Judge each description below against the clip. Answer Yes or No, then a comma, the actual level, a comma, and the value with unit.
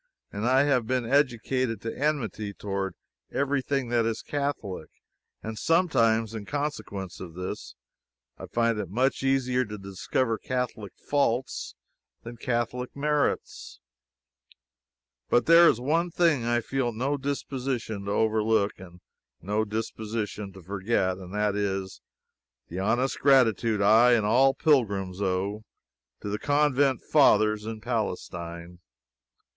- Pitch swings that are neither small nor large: Yes, average, 4.6 semitones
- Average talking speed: No, slow, 130 wpm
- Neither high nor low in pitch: No, low, 115 Hz